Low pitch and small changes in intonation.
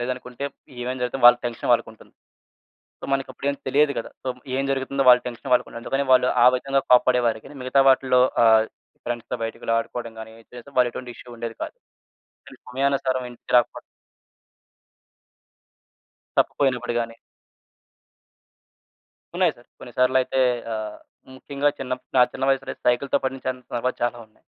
Yes: low, 125 Hz; narrow, 2.0 semitones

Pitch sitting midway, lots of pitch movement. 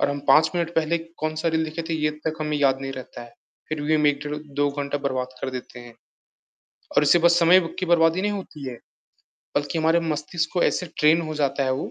No: medium, 150 Hz; average, 2.7 semitones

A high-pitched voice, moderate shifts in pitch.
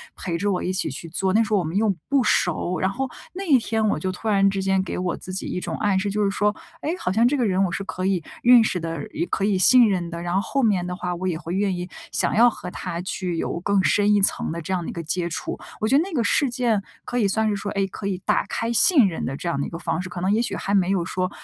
Yes: high, 195 Hz; average, 3.3 semitones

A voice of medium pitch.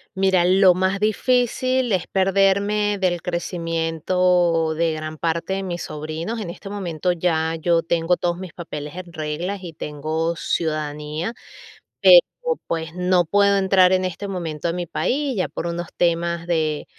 Yes: medium, 175 Hz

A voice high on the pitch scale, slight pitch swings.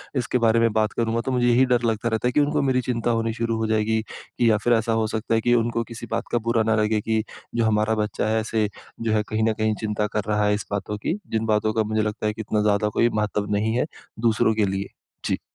No: low, 110 Hz; narrow, 1.5 semitones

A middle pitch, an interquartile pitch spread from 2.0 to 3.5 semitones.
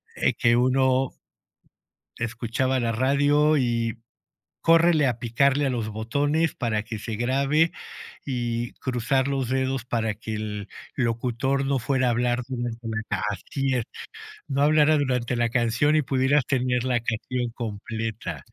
No: low, 125 Hz; average, 2.9 semitones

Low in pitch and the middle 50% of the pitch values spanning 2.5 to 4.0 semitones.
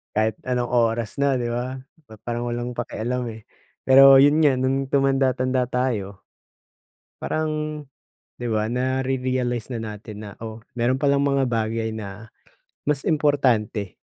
Yes: low, 125 Hz; average, 3.1 semitones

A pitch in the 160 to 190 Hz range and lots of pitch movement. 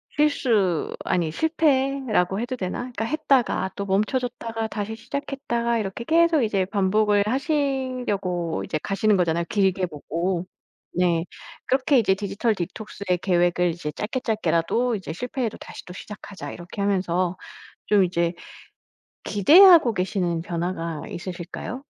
No: high, 205 Hz; wide, 5.7 semitones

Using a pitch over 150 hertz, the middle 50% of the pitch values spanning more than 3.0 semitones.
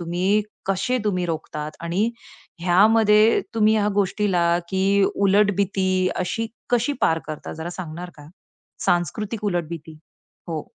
Yes: high, 190 Hz; average, 3.6 semitones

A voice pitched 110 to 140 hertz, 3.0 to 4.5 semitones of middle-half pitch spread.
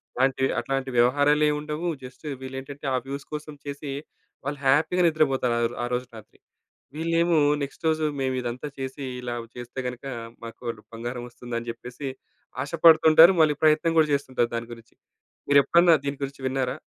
Yes: low, 135 Hz; average, 3.6 semitones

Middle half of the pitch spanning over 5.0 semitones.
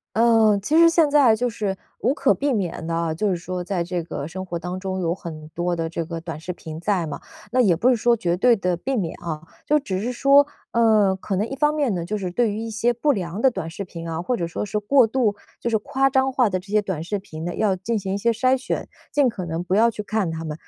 Yes: wide, 5.5 semitones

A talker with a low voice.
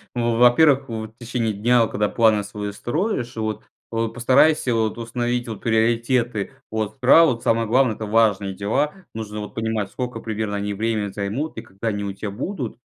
Yes: low, 115 Hz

